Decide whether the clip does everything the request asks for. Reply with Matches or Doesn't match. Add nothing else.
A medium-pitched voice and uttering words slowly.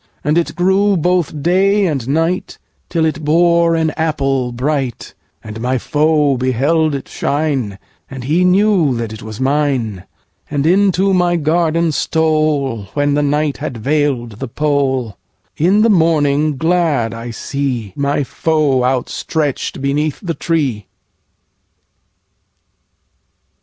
Matches